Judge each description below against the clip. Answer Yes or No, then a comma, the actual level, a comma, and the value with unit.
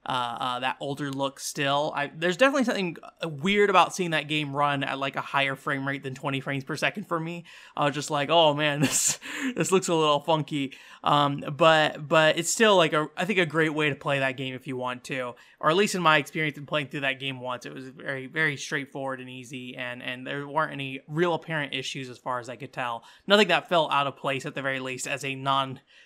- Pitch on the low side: No, medium, 145 Hz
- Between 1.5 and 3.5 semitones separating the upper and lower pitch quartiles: Yes, average, 2.9 semitones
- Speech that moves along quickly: Yes, fast, 245 wpm